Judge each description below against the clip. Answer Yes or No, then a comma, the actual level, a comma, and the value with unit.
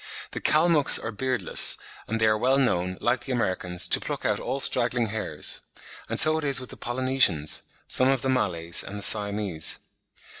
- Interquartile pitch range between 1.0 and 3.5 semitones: No, average, 5.3 semitones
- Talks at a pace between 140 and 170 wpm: No, average, 185 wpm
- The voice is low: Yes, low, 120 Hz